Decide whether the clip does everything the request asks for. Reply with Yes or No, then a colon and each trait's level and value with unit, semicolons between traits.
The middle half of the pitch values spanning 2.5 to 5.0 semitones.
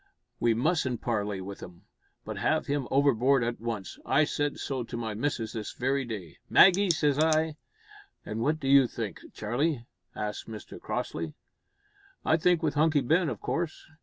No: wide, 5.5 semitones